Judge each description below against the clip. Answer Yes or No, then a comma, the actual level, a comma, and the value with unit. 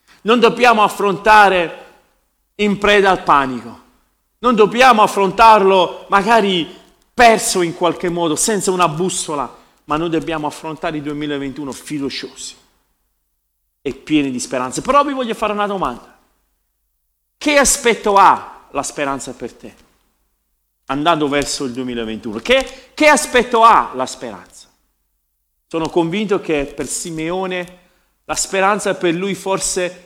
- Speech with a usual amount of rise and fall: No, wide, 6.1 semitones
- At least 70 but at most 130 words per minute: Yes, average, 125 wpm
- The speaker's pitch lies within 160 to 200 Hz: Yes, medium, 180 Hz